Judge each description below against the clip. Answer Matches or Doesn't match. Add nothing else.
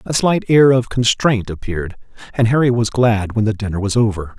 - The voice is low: Matches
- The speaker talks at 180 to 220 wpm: Matches